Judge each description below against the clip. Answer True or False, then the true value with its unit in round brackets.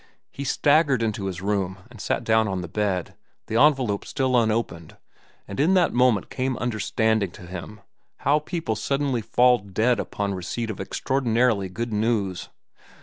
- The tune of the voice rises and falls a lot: False (4.4 semitones)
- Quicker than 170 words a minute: False (155 wpm)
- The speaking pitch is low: True (110 Hz)